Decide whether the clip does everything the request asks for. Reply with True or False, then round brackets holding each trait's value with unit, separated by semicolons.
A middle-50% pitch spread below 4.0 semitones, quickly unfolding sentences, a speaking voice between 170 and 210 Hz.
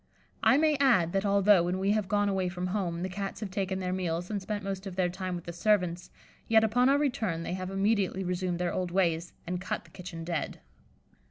True (2.4 semitones; 230 wpm; 190 Hz)